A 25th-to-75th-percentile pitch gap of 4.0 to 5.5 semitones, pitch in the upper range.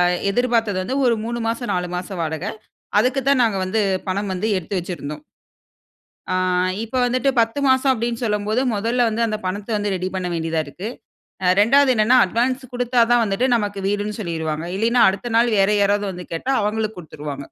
Yes: average, 4.5 semitones; high, 210 Hz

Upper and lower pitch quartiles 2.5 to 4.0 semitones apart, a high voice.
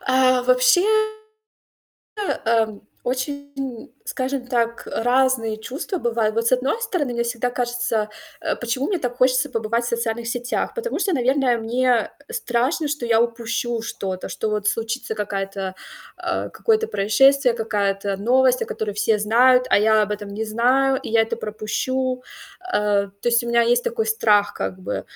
Yes: average, 3.0 semitones; high, 235 Hz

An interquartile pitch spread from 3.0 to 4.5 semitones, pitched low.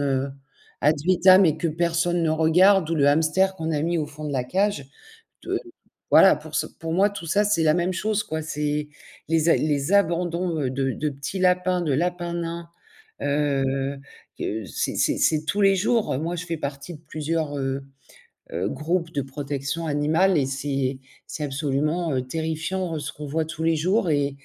No: average, 3.5 semitones; medium, 160 Hz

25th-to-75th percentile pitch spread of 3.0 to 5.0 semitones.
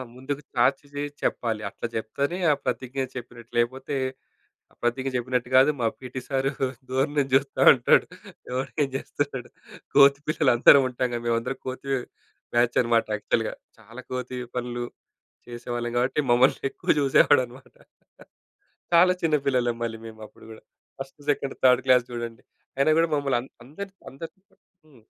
No: narrow, 2.6 semitones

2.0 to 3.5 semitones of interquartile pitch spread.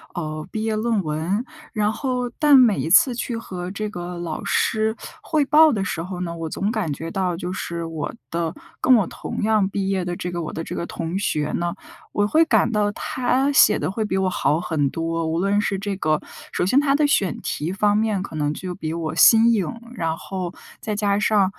No: average, 4.4 semitones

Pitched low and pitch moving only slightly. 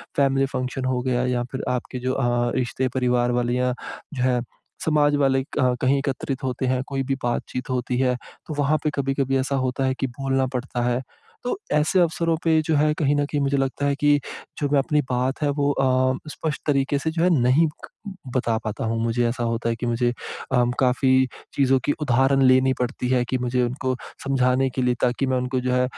Yes: low, 130 Hz; narrow, 1.8 semitones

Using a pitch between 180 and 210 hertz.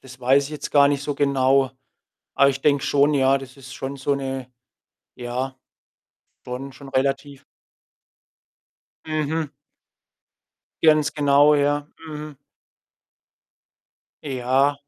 No: medium, 140 Hz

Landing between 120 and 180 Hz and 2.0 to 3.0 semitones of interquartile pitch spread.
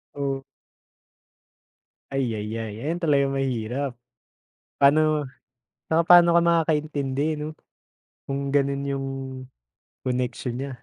Yes: medium, 140 Hz; average, 2.7 semitones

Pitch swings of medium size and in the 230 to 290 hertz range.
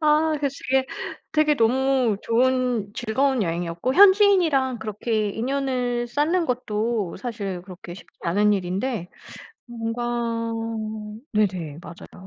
Yes: average, 4.5 semitones; high, 240 Hz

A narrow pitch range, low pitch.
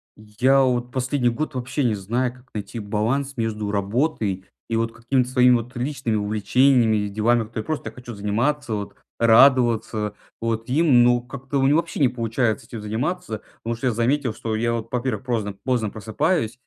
No: average, 3.0 semitones; low, 120 Hz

